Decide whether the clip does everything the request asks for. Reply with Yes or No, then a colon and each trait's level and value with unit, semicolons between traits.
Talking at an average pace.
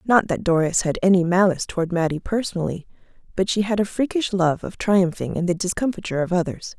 Yes: average, 195 wpm